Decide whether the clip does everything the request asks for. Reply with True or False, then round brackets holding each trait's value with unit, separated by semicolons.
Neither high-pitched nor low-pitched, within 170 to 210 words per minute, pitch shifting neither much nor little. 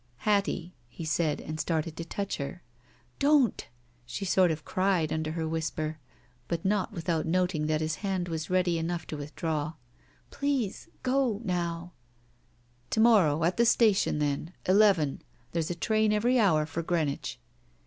True (170 Hz; 175 wpm; 4.1 semitones)